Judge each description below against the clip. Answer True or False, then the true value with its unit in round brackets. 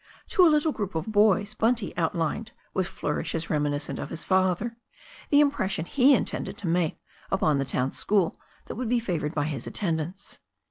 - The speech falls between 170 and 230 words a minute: True (180 wpm)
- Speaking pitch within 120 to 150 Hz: False (185 Hz)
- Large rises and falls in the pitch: True (5.8 semitones)